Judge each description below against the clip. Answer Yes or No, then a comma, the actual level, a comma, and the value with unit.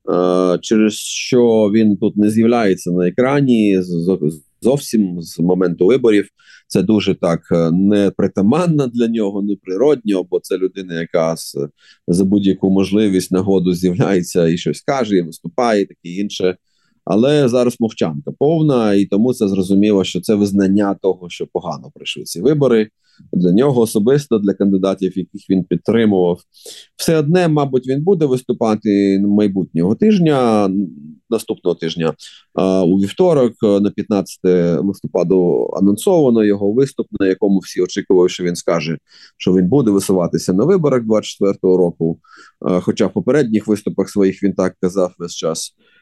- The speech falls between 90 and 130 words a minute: No, average, 140 wpm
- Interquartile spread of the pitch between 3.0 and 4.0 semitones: Yes, average, 3.3 semitones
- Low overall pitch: Yes, low, 100 Hz